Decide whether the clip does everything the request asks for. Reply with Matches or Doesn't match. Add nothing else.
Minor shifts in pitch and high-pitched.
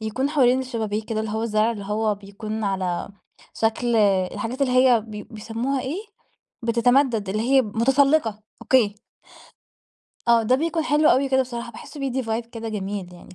Doesn't match